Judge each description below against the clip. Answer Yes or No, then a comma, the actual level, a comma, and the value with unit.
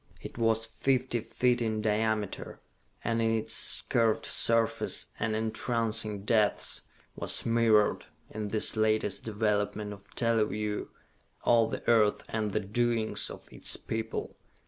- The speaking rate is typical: No, slow, 125 wpm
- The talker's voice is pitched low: Yes, low, 110 Hz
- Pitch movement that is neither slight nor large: No, narrow, 1.4 semitones